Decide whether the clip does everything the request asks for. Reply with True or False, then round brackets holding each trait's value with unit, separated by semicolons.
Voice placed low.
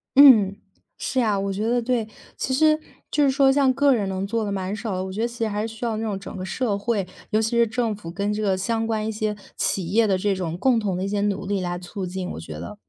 False (210 Hz)